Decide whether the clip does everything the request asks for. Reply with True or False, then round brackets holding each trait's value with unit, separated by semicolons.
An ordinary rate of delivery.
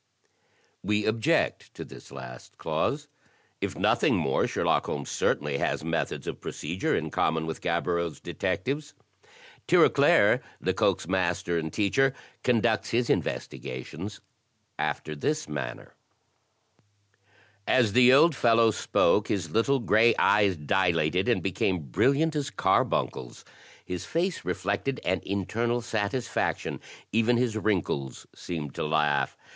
False (120 wpm)